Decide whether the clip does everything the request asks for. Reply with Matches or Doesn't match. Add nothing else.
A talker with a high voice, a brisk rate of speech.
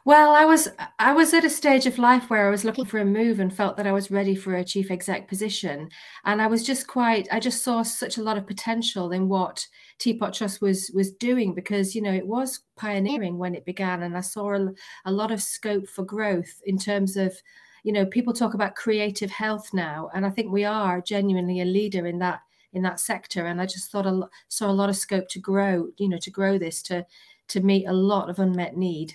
Matches